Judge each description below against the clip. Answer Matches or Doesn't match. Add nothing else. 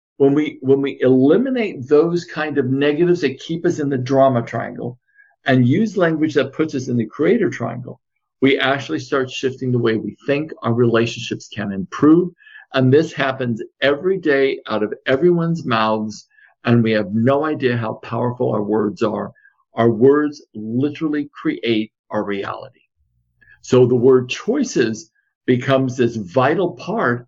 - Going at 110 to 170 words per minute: Matches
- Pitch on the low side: Matches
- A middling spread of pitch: Matches